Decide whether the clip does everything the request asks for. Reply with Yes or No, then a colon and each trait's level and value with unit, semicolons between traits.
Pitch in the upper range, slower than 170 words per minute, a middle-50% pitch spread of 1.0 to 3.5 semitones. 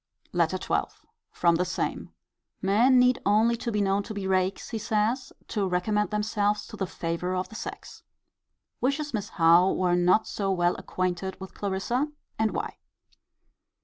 Yes: high, 200 Hz; average, 155 wpm; average, 3.1 semitones